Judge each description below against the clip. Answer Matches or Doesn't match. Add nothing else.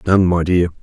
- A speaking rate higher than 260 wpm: Doesn't match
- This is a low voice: Matches